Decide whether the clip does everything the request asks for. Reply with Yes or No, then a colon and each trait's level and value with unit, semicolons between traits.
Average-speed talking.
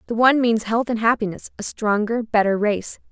Yes: average, 175 wpm